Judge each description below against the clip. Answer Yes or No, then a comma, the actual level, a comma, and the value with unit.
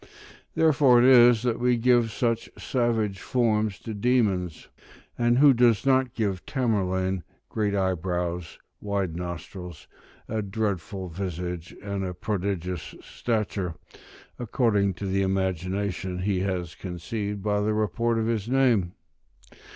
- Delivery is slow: Yes, slow, 125 wpm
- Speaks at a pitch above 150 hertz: No, low, 100 Hz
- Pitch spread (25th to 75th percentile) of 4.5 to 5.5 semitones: No, average, 4.1 semitones